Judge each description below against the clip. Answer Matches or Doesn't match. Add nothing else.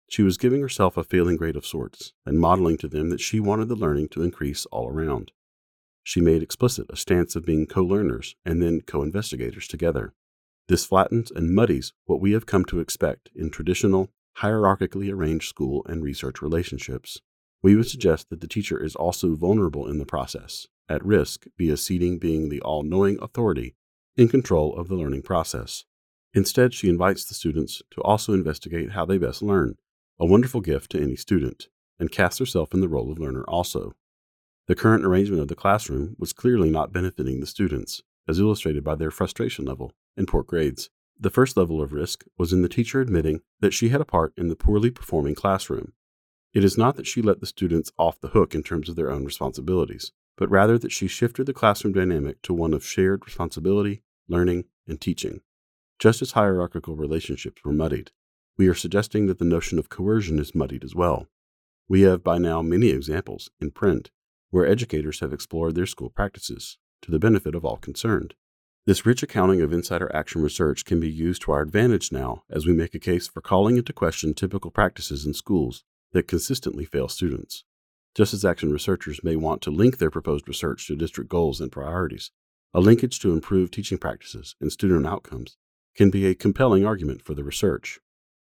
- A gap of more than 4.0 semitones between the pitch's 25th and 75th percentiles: Matches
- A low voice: Matches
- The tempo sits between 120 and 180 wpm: Doesn't match